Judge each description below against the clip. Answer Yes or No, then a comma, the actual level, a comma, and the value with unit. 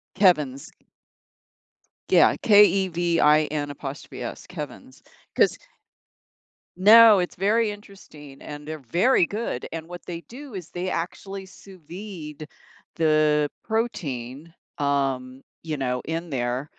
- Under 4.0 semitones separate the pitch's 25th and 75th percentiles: No, average, 4.9 semitones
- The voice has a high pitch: No, medium, 165 Hz